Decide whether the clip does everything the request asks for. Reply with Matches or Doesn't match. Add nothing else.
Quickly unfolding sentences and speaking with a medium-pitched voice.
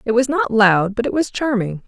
Doesn't match